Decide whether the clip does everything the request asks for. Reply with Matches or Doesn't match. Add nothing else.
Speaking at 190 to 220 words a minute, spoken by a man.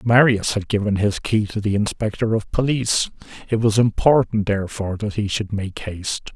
Doesn't match